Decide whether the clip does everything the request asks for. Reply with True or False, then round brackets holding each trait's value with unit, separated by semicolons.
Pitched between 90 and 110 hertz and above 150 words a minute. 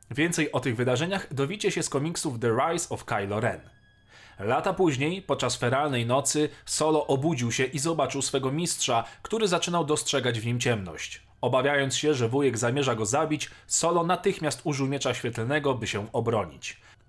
False (140 Hz; 160 wpm)